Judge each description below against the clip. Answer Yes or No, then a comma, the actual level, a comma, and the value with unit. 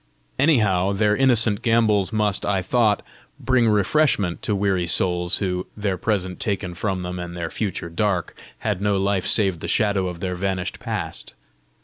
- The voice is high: No, low, 100 Hz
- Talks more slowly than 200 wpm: Yes, average, 160 wpm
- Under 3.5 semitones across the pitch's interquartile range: Yes, average, 2.8 semitones